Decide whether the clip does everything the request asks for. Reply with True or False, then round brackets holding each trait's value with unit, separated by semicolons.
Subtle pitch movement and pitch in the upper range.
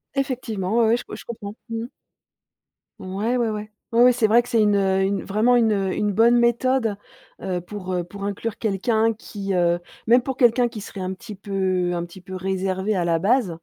False (3.7 semitones; 210 Hz)